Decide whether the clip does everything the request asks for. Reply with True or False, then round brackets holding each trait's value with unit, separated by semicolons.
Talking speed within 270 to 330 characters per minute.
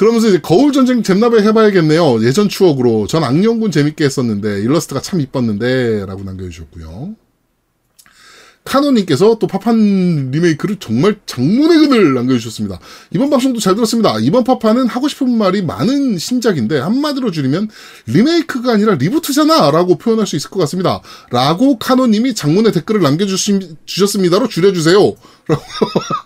False (385 characters per minute)